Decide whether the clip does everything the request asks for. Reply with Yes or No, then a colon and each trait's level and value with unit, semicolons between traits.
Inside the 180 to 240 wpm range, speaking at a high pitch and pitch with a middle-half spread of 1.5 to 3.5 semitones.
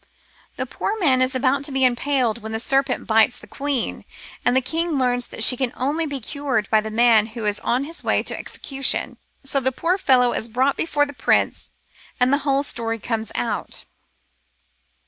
Yes: average, 195 wpm; very high, 255 Hz; average, 3.1 semitones